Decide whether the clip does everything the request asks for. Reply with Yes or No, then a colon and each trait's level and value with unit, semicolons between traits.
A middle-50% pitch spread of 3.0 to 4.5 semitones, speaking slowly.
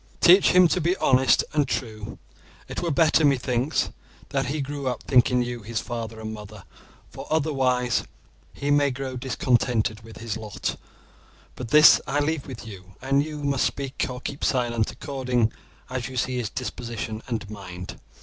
No: average, 3.7 semitones; average, 170 wpm